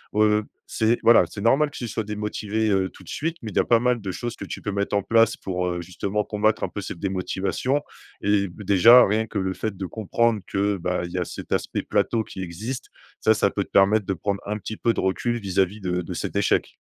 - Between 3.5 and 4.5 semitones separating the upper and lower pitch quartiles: No, average, 2.7 semitones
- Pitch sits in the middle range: No, low, 105 Hz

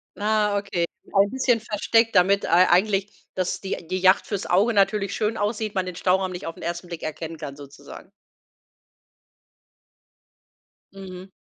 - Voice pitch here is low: No, high, 195 Hz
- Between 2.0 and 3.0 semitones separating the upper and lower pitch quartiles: Yes, average, 2.7 semitones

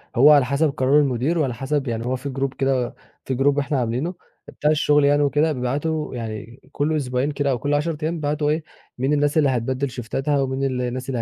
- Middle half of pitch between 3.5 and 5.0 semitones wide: No, narrow, 2.6 semitones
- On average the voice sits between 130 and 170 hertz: Yes, medium, 140 Hz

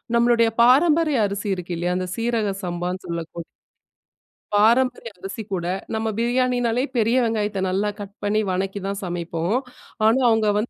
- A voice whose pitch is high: Yes, high, 215 Hz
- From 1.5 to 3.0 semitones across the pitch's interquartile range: No, average, 4.3 semitones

